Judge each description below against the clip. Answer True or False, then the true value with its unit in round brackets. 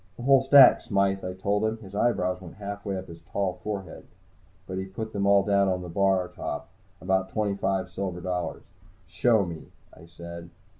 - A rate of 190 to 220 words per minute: True (195 wpm)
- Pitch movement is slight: True (1.8 semitones)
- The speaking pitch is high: False (95 Hz)